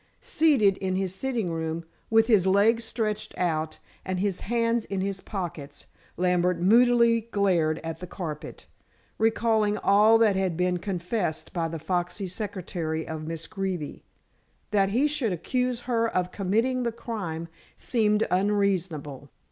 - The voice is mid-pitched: No, high, 195 Hz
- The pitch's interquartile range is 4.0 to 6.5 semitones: Yes, average, 4.4 semitones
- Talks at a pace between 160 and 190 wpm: No, average, 140 wpm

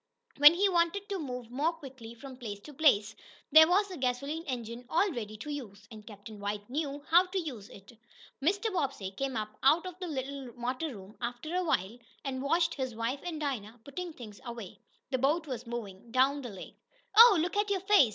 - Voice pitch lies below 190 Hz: No, very high, 270 Hz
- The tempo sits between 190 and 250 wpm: Yes, fast, 205 wpm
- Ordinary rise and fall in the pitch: No, wide, 6.1 semitones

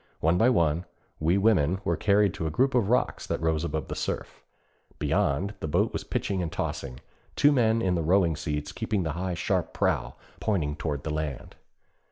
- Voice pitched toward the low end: Yes, very low, 85 Hz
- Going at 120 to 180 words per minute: No, average, 195 wpm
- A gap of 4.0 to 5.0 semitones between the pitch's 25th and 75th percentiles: Yes, average, 4.5 semitones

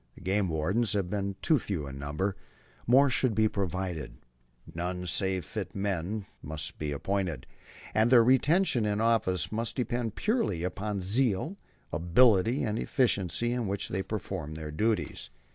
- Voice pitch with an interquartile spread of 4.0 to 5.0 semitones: Yes, average, 4.6 semitones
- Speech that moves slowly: No, average, 155 wpm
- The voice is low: Yes, low, 100 Hz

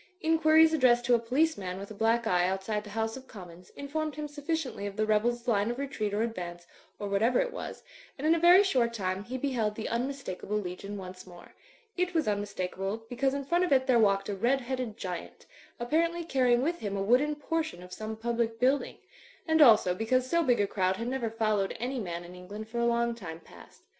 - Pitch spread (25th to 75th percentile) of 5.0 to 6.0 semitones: Yes, average, 5.3 semitones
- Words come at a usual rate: No, fast, 220 wpm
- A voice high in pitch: Yes, high, 235 Hz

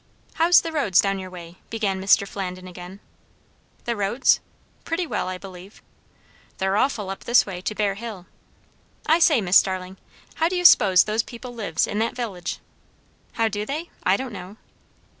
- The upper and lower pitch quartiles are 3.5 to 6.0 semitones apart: Yes, average, 4.3 semitones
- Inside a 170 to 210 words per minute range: Yes, average, 175 wpm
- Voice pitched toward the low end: No, high, 200 Hz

